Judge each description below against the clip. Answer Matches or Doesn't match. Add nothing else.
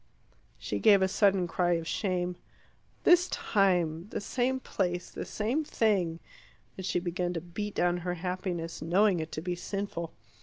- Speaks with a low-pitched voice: Doesn't match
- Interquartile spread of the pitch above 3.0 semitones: Doesn't match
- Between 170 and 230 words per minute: Doesn't match